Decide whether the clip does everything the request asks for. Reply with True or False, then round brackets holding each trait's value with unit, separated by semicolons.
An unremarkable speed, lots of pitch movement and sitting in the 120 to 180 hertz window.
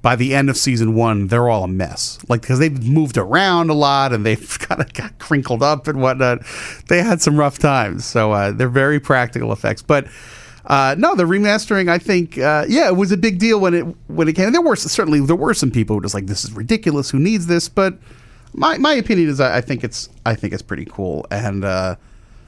False (240 wpm; 6.5 semitones; 135 Hz)